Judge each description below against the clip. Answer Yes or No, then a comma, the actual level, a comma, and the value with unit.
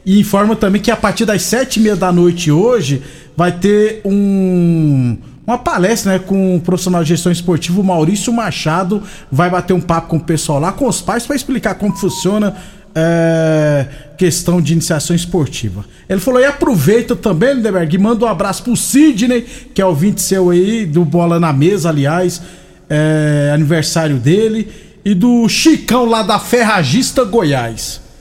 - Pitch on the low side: No, medium, 185 Hz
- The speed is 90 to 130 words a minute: No, average, 175 wpm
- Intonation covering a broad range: No, average, 4.6 semitones